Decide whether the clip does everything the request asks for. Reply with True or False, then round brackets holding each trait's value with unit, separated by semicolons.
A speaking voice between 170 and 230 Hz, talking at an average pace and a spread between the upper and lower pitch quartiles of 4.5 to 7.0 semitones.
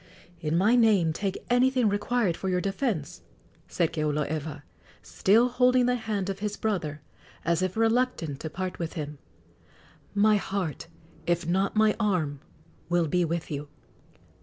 True (185 Hz; 145 wpm; 5.2 semitones)